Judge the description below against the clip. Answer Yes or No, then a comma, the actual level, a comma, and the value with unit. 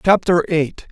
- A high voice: No, medium, 165 Hz